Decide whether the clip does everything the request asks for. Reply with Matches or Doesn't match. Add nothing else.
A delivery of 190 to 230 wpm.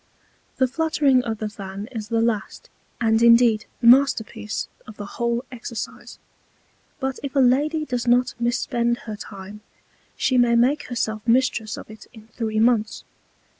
Doesn't match